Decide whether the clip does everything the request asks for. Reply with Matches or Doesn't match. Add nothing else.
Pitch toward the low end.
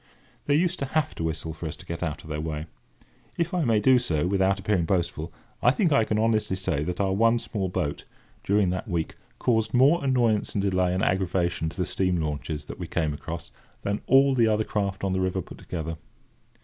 Matches